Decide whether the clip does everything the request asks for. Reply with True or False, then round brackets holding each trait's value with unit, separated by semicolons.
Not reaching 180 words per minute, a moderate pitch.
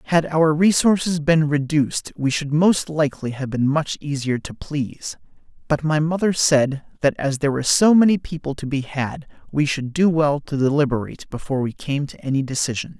False (190 wpm; 145 Hz)